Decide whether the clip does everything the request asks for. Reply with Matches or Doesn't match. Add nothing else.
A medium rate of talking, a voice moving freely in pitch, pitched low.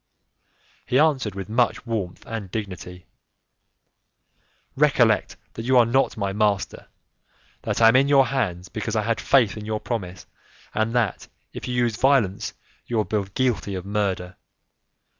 Doesn't match